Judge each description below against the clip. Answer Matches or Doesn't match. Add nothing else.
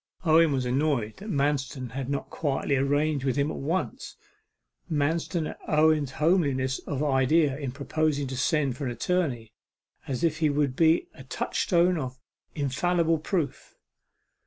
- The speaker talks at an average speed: Matches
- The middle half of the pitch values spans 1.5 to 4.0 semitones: Matches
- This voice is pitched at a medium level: Matches